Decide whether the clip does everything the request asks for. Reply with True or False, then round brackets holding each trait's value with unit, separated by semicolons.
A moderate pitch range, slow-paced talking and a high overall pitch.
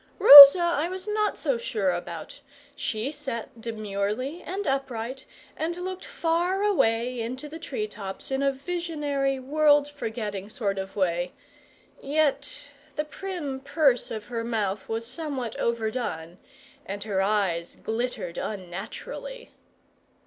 False (6.1 semitones; 125 wpm; 255 Hz)